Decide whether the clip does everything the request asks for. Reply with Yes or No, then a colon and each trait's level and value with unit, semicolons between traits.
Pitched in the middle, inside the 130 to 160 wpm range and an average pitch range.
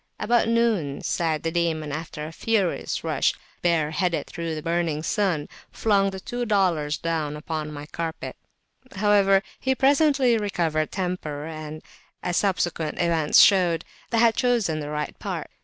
Yes: medium, 170 Hz; average, 150 wpm; average, 4.8 semitones